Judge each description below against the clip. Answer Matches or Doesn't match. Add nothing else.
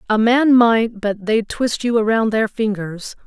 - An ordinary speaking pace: Matches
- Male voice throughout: Doesn't match